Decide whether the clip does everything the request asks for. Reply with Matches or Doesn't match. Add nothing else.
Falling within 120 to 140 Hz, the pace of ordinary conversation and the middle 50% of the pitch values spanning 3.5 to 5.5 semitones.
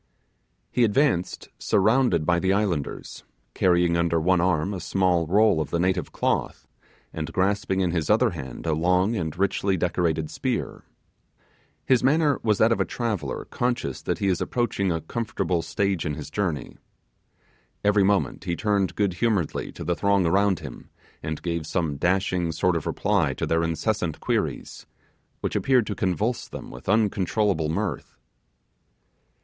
Doesn't match